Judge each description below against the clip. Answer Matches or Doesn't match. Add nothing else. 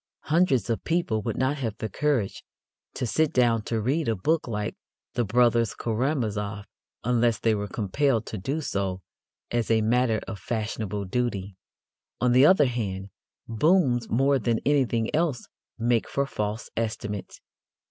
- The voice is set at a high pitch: Doesn't match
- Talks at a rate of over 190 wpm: Doesn't match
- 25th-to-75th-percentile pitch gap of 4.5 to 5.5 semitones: Doesn't match